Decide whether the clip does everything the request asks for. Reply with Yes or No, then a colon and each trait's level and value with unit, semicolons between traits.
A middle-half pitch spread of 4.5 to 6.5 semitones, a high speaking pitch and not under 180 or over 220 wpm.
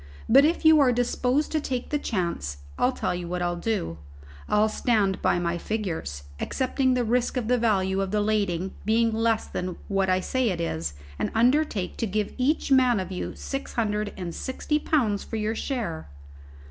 Yes: average, 5.3 semitones; high, 215 Hz; average, 190 wpm